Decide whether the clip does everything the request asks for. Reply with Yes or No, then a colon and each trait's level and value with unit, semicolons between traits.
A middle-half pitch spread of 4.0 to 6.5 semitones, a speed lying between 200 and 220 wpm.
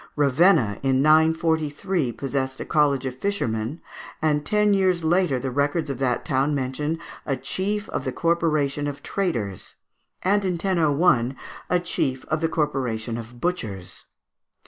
No: average, 4.6 semitones; average, 145 wpm